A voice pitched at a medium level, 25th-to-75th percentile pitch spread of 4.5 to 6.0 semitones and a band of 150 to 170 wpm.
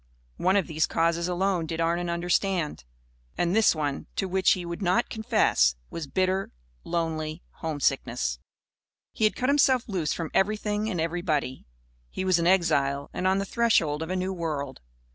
No: medium, 175 Hz; average, 3.4 semitones; average, 165 wpm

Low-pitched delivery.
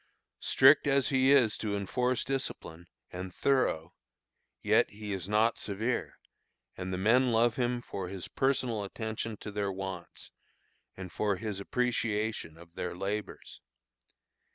Yes: low, 105 Hz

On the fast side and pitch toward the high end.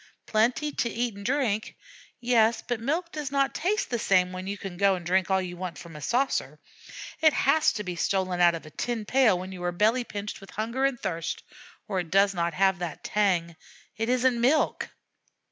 Yes: fast, 210 wpm; high, 205 Hz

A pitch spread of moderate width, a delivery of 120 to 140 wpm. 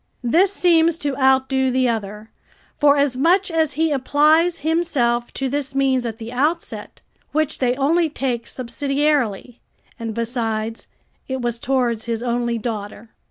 Yes: average, 4.1 semitones; slow, 135 wpm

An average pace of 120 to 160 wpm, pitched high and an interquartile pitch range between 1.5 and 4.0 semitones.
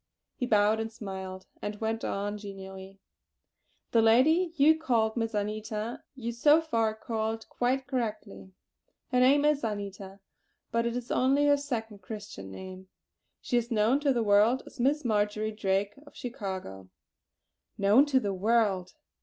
Yes: average, 150 wpm; high, 220 Hz; average, 3.6 semitones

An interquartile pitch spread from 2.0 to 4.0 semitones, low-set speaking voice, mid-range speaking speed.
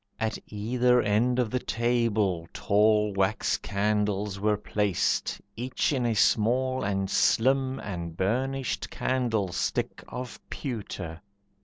No: average, 3.6 semitones; low, 110 Hz; slow, 115 wpm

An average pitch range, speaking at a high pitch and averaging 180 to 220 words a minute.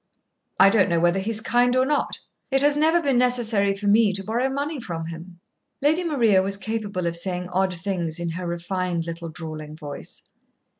No: wide, 6.0 semitones; high, 195 Hz; average, 195 wpm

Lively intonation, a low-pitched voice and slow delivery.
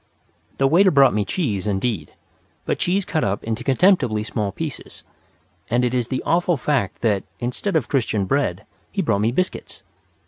No: wide, 6.8 semitones; low, 125 Hz; average, 170 wpm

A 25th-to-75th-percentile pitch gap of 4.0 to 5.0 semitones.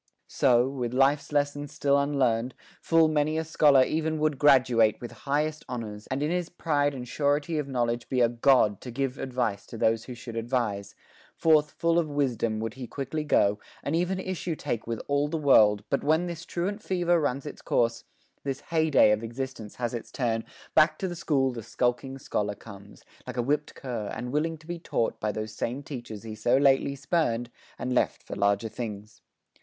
Yes: average, 4.4 semitones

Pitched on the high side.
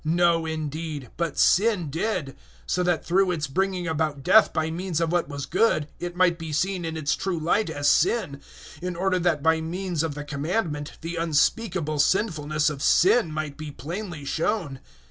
No: medium, 165 Hz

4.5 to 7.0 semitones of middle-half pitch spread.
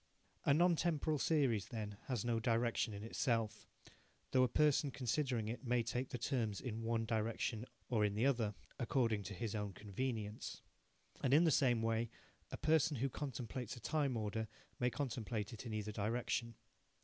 No: average, 3.3 semitones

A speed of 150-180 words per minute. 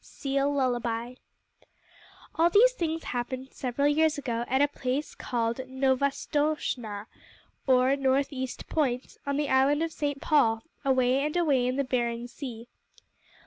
No: average, 140 wpm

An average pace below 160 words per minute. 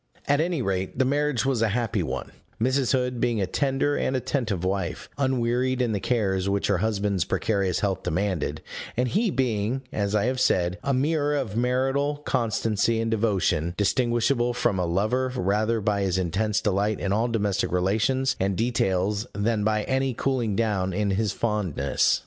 No: average, 170 wpm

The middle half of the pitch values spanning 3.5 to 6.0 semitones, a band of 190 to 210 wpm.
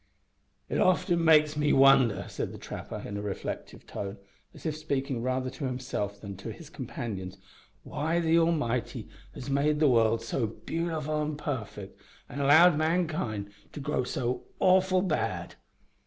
No: average, 5.0 semitones; average, 155 wpm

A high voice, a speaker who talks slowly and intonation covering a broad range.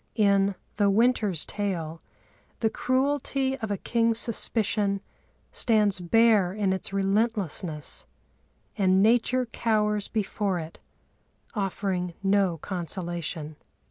No: high, 200 Hz; slow, 100 wpm; average, 3.4 semitones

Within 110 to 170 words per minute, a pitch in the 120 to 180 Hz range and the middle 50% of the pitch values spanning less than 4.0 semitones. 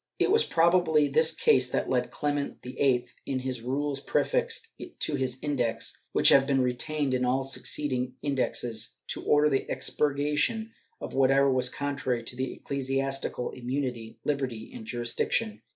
Yes: average, 150 wpm; low, 135 Hz; narrow, 2.5 semitones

